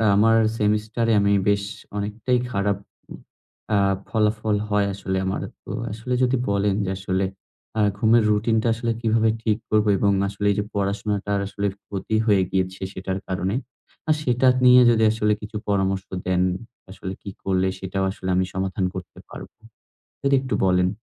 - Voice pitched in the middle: No, low, 105 Hz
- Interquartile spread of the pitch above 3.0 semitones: No, narrow, 2.5 semitones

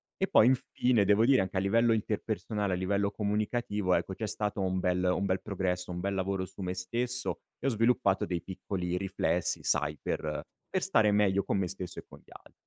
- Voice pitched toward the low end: Yes, low, 100 Hz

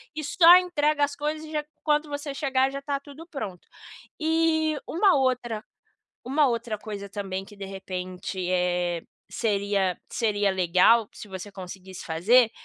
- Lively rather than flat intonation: Yes, wide, 7.5 semitones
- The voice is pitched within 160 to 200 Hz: No, high, 230 Hz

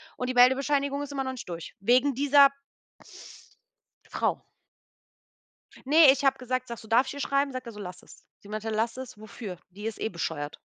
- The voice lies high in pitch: Yes, very high, 250 Hz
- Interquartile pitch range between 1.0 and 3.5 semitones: No, average, 4.2 semitones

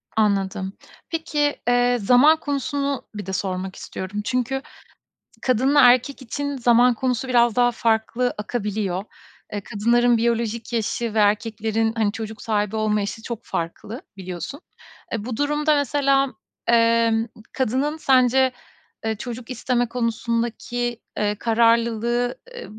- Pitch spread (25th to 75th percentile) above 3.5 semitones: No, average, 2.8 semitones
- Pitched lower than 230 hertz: No, high, 235 Hz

